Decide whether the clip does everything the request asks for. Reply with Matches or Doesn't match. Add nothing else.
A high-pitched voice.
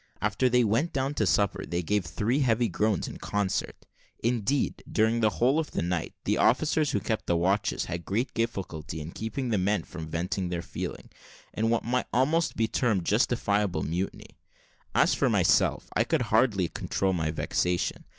Doesn't match